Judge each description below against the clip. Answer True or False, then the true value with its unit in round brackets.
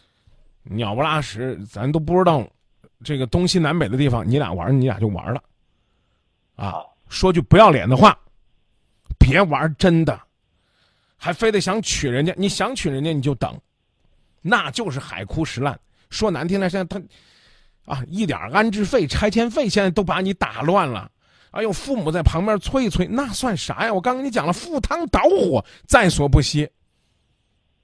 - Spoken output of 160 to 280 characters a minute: True (240 characters per minute)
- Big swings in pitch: True (6.4 semitones)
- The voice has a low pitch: False (175 Hz)